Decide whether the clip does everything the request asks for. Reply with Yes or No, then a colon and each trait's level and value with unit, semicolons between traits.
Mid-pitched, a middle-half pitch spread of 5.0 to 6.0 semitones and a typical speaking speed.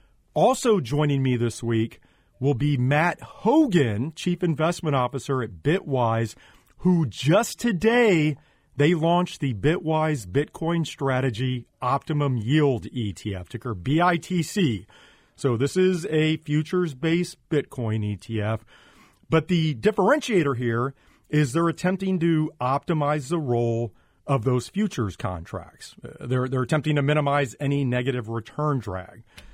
No: medium, 145 Hz; average, 5.3 semitones; slow, 120 wpm